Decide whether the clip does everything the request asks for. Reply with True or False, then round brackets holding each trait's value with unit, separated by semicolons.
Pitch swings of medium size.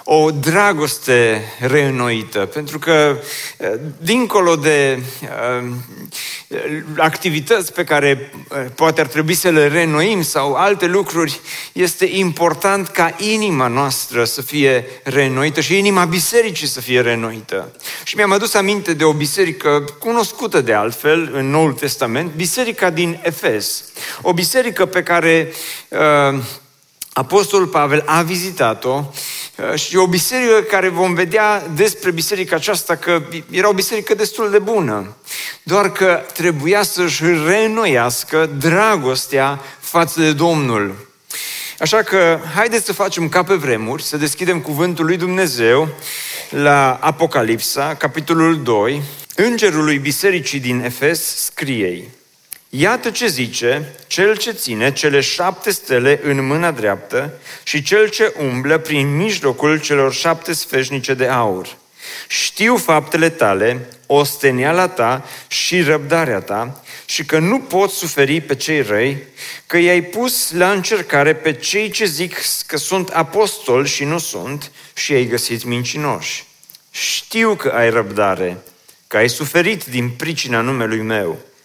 True (5.0 semitones)